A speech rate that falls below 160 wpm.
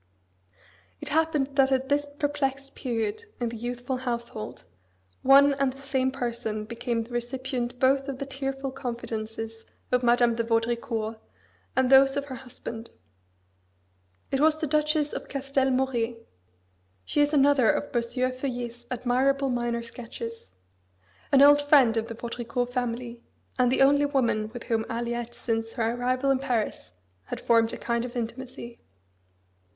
Yes: average, 150 wpm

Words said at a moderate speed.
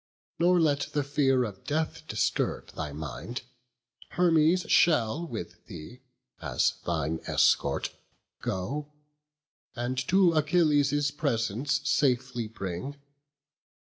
No: slow, 100 wpm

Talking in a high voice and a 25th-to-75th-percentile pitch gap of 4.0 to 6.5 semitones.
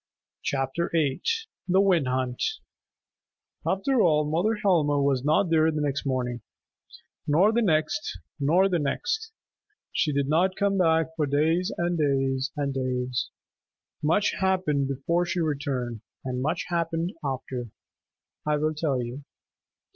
No: medium, 150 Hz; average, 4.3 semitones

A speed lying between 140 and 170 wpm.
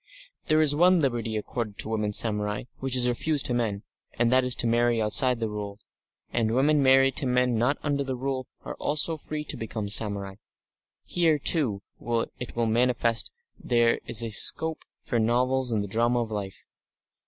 No: average, 180 wpm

